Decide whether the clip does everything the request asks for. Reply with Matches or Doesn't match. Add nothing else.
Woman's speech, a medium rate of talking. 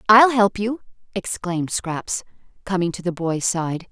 Matches